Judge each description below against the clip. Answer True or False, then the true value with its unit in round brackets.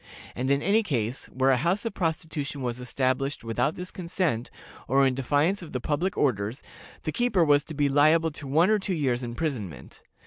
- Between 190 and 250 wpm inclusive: True (195 wpm)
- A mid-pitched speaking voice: True (145 Hz)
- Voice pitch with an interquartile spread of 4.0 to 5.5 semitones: True (4.7 semitones)